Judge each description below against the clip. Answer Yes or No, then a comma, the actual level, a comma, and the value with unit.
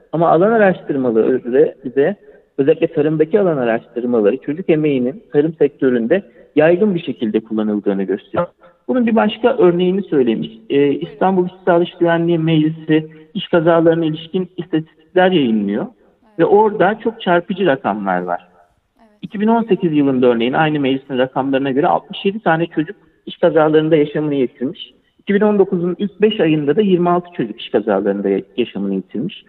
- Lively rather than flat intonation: Yes, wide, 5.9 semitones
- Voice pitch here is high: No, medium, 160 Hz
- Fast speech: No, average, 130 wpm